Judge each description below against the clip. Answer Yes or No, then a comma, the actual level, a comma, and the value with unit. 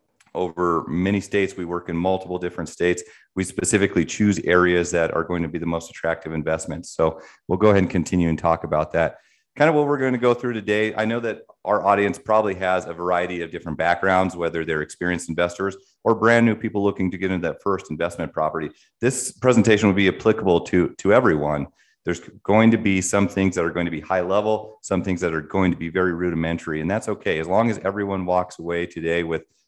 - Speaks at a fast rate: Yes, fast, 220 wpm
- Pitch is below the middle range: Yes, very low, 90 Hz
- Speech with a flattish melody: No, average, 3.2 semitones